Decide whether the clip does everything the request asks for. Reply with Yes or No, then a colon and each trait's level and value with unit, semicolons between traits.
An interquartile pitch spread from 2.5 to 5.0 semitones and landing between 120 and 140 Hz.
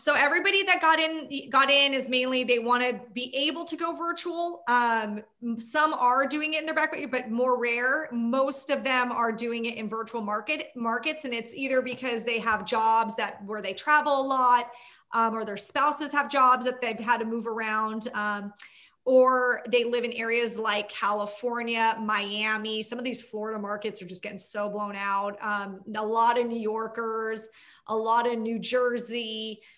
No: average, 3.1 semitones; high, 235 Hz